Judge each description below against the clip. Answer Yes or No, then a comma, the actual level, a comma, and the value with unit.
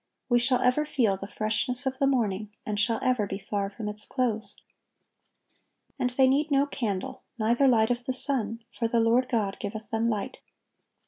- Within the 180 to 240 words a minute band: Yes, average, 185 wpm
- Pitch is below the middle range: No, high, 230 Hz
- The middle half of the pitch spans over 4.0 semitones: No, average, 3.3 semitones